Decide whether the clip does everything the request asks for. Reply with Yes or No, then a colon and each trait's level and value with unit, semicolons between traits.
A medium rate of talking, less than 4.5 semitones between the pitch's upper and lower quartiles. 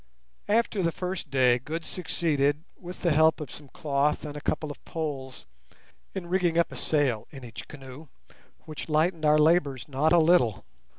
Yes: average, 175 wpm; average, 3.3 semitones